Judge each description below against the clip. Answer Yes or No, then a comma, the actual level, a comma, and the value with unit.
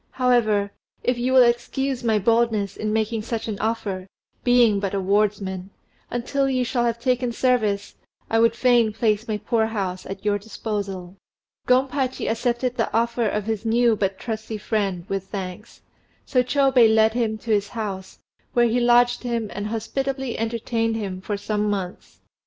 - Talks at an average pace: Yes, average, 165 wpm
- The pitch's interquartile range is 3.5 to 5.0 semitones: No, average, 2.8 semitones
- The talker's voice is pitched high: Yes, high, 225 Hz